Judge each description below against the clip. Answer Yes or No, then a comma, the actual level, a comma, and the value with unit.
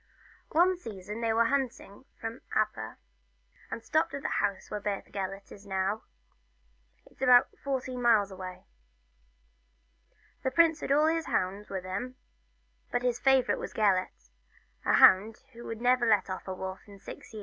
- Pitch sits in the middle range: No, high, 225 Hz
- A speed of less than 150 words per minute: No, average, 165 wpm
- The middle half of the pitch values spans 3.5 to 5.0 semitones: Yes, average, 4.6 semitones